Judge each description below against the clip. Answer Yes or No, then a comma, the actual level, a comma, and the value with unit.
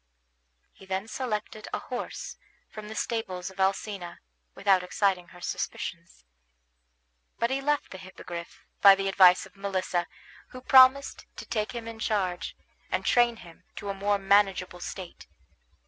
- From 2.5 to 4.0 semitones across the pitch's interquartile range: Yes, average, 3.3 semitones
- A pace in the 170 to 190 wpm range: No, average, 145 wpm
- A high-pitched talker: Yes, high, 195 Hz